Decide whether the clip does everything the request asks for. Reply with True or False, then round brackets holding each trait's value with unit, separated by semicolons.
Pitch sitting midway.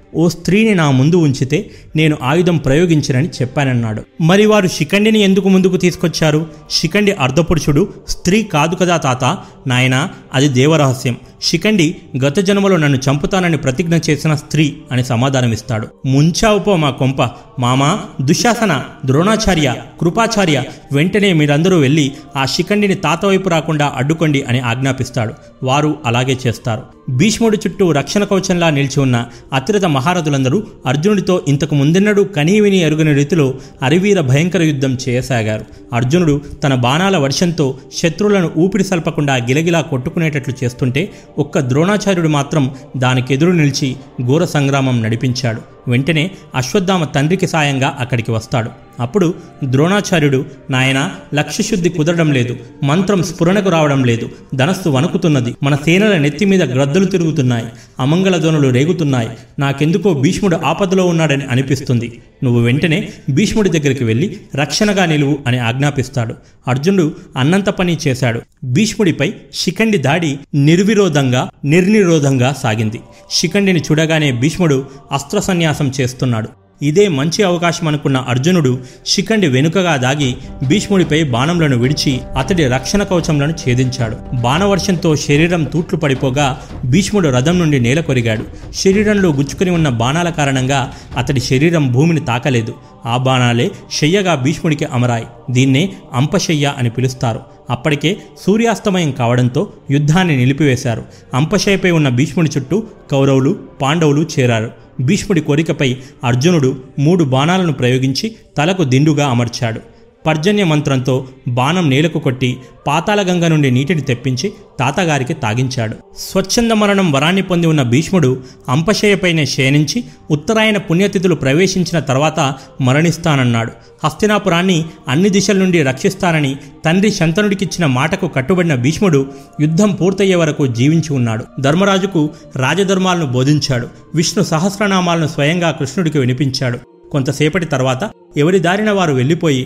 True (150 Hz)